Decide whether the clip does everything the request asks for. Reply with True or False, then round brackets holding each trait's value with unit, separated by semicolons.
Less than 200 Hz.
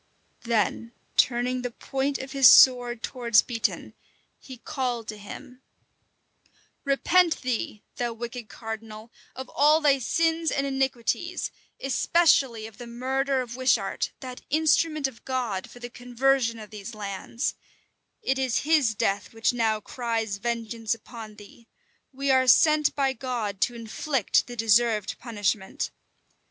False (245 Hz)